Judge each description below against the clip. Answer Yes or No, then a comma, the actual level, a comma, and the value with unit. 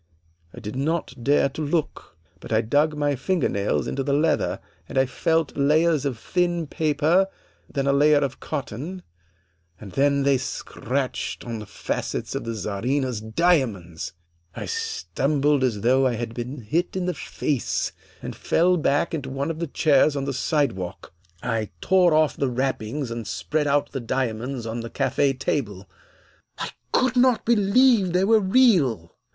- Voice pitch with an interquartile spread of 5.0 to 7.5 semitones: Yes, average, 5.3 semitones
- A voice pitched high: No, medium, 140 Hz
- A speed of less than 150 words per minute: No, average, 165 wpm